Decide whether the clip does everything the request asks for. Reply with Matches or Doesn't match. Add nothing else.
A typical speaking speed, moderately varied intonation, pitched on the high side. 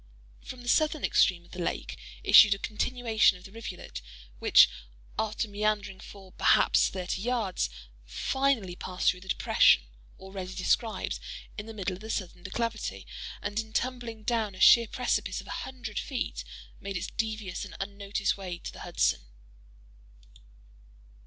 Matches